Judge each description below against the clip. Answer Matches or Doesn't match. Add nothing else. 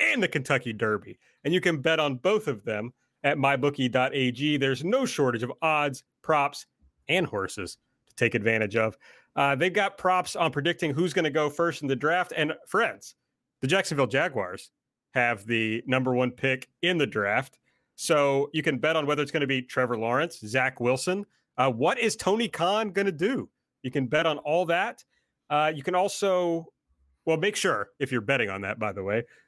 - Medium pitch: Matches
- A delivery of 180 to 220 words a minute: Matches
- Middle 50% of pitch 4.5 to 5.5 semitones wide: Matches